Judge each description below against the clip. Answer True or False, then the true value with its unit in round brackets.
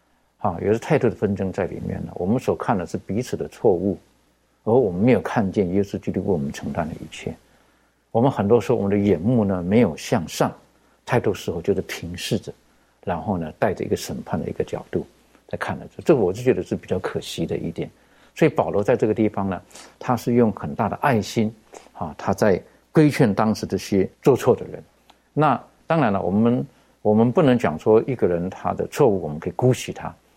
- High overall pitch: False (110 Hz)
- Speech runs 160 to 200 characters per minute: False (310 characters per minute)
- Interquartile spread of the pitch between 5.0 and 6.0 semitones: False (3.5 semitones)